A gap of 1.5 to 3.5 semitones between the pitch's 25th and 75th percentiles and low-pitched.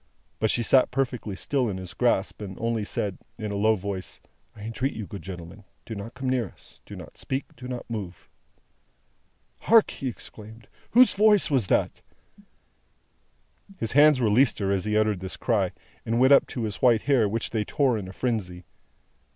No: average, 4.1 semitones; low, 110 Hz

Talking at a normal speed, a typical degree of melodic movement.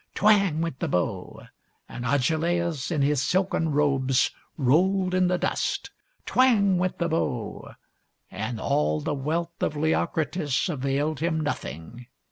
No: slow, 130 wpm; average, 4.5 semitones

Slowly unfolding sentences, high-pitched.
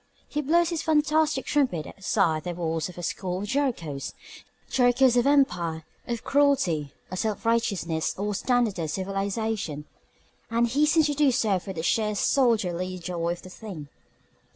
No: average, 155 wpm; high, 210 Hz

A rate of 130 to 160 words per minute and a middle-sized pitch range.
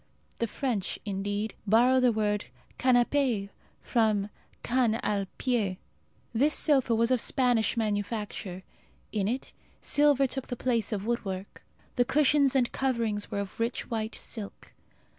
Yes: slow, 135 wpm; average, 3.6 semitones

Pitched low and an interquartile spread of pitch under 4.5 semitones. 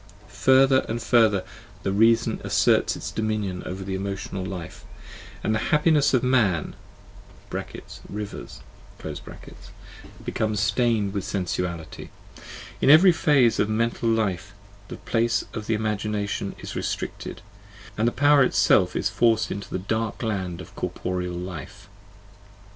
Yes: low, 110 Hz; average, 3.2 semitones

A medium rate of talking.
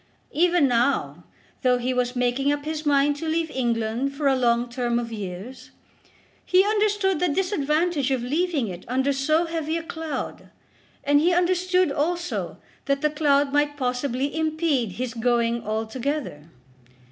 Yes: average, 150 wpm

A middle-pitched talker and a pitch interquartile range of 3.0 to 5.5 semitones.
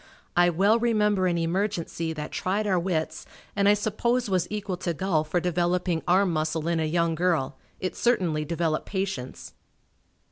Yes: medium, 180 Hz; average, 3.3 semitones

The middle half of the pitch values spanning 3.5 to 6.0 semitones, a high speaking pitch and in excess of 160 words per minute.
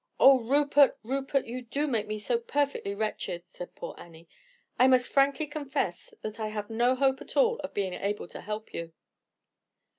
Yes: average, 4.8 semitones; high, 240 Hz; average, 180 wpm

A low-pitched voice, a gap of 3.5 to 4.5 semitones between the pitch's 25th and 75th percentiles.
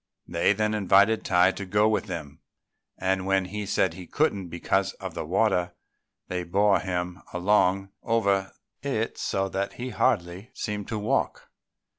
No: very low, 95 Hz; narrow, 2.6 semitones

